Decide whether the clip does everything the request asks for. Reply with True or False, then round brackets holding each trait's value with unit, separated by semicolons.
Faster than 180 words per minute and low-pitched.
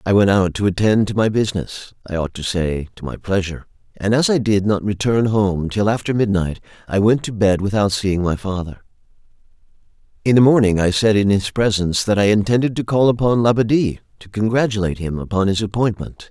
True (200 wpm; 105 Hz)